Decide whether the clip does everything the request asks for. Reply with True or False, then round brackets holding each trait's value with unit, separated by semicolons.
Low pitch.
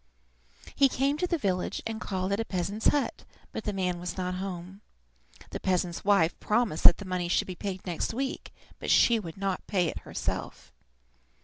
False (190 Hz)